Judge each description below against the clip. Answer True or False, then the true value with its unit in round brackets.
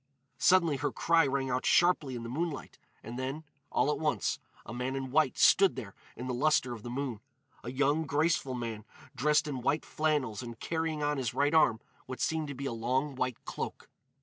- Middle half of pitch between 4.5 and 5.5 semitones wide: False (3.5 semitones)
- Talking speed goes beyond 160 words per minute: True (200 wpm)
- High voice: False (135 Hz)